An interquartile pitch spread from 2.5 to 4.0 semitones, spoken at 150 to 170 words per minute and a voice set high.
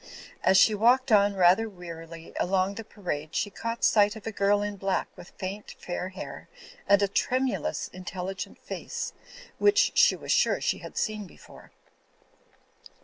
Yes: average, 2.8 semitones; average, 155 wpm; high, 200 Hz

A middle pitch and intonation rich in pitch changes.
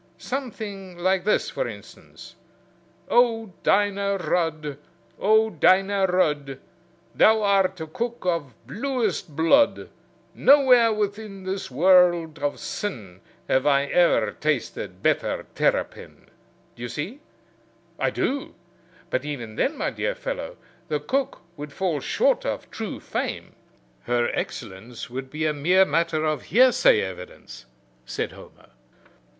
Yes: medium, 180 Hz; wide, 6.5 semitones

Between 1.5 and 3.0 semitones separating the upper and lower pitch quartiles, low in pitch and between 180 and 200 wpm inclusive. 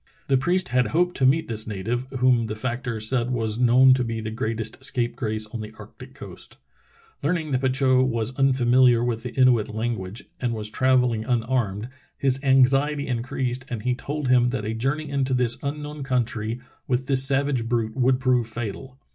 Yes: narrow, 2.5 semitones; low, 125 Hz; average, 185 wpm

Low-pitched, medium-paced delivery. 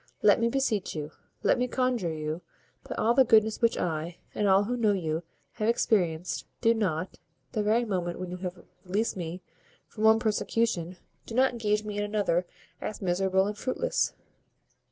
No: high, 205 Hz; average, 180 wpm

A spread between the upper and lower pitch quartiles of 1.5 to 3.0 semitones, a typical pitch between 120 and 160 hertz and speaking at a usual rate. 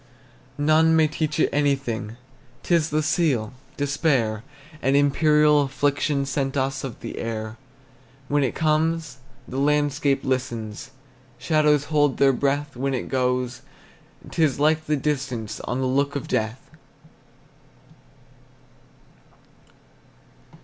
No: average, 2.7 semitones; medium, 140 Hz; slow, 120 wpm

